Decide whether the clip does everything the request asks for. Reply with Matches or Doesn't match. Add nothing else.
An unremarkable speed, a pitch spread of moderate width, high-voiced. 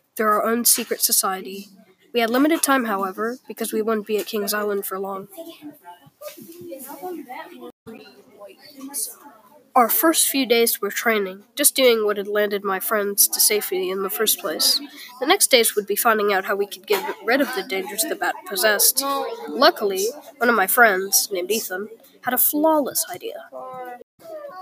Doesn't match